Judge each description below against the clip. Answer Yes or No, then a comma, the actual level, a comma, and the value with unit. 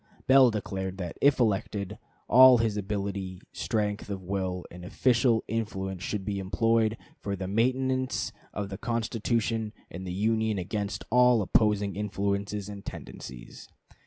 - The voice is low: Yes, low, 105 Hz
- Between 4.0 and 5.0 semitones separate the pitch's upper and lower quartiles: No, average, 2.8 semitones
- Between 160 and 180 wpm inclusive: No, slow, 135 wpm